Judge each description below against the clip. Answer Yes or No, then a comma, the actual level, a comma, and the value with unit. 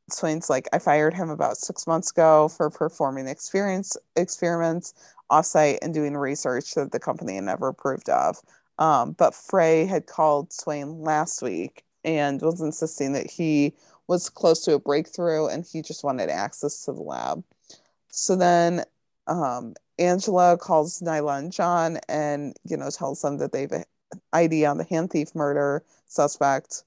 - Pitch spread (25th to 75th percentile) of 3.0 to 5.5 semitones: No, narrow, 2.6 semitones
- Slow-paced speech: No, average, 165 wpm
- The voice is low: No, medium, 155 Hz